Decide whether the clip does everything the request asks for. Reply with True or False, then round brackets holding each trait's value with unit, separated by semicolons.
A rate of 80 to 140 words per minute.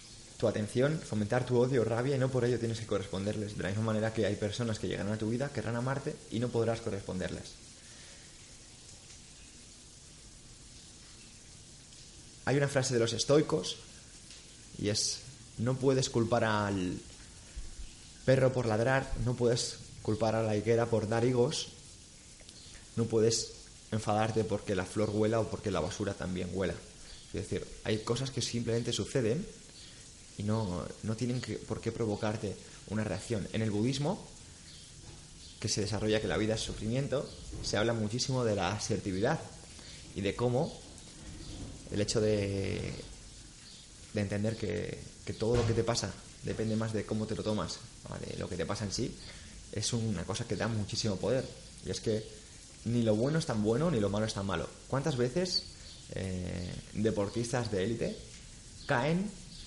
False (160 wpm)